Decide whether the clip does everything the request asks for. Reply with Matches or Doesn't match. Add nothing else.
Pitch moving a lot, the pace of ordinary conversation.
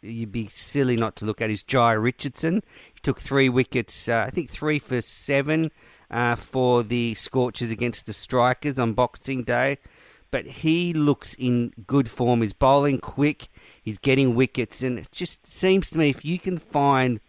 Doesn't match